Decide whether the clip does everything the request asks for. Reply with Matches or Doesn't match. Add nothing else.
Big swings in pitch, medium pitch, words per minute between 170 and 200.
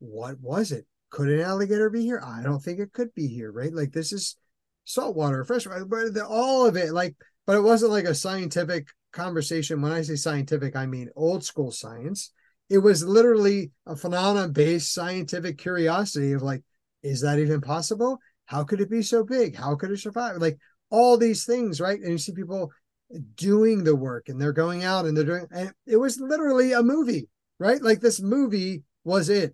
Matches